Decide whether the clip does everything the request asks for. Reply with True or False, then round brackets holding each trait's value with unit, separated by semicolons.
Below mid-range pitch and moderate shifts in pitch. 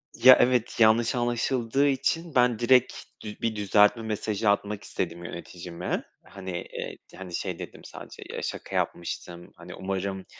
True (110 Hz; 4.2 semitones)